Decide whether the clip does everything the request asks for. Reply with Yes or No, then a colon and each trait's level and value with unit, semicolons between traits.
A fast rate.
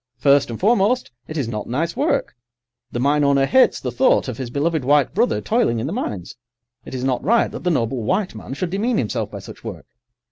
Yes: fast, 220 wpm